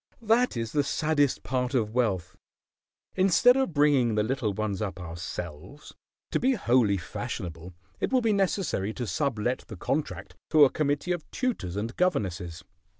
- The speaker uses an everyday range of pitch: No, wide, 8.2 semitones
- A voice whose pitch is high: No, low, 125 Hz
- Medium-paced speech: Yes, average, 155 wpm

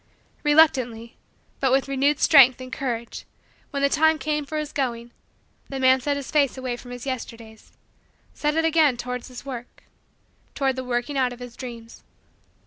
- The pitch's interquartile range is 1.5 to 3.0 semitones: Yes, average, 2.7 semitones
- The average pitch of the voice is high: Yes, very high, 260 Hz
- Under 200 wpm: Yes, average, 170 wpm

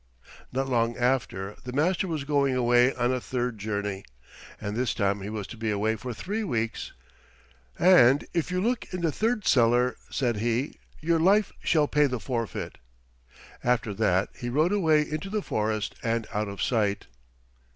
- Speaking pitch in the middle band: No, low, 125 Hz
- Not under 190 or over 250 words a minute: No, average, 170 wpm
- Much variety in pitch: Yes, wide, 5.7 semitones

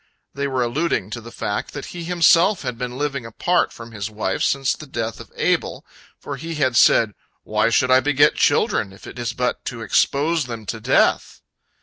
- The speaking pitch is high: No, low, 125 Hz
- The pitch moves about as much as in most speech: Yes, average, 4.2 semitones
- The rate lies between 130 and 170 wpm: No, average, 200 wpm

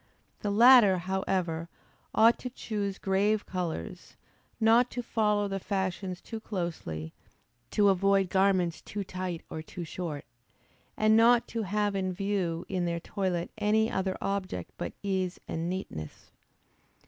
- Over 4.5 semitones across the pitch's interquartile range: No, average, 2.9 semitones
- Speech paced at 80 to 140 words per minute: Yes, slow, 135 wpm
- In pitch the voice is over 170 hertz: Yes, high, 190 Hz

